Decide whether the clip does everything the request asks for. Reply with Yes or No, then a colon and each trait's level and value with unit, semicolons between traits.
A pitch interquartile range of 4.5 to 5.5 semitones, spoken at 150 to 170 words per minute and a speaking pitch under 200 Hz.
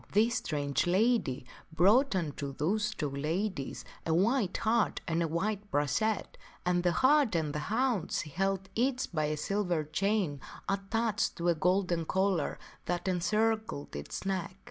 Yes: average, 5.2 semitones; average, 155 wpm; medium, 185 Hz